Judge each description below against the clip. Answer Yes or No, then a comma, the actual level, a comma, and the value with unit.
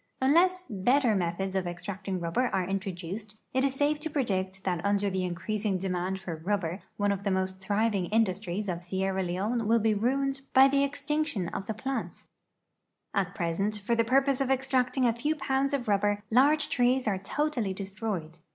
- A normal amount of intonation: No, wide, 5.7 semitones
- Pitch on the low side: No, high, 205 Hz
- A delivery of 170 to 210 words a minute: Yes, average, 180 wpm